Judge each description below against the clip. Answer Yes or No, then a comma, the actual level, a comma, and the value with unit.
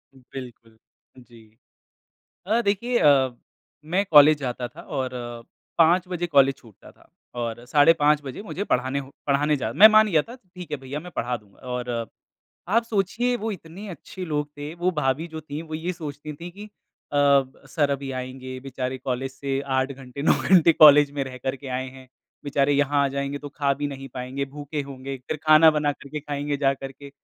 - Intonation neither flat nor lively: Yes, average, 3.5 semitones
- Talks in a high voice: No, medium, 145 Hz